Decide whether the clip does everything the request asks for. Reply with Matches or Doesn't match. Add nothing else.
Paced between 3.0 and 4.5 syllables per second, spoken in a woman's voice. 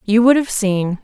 Matches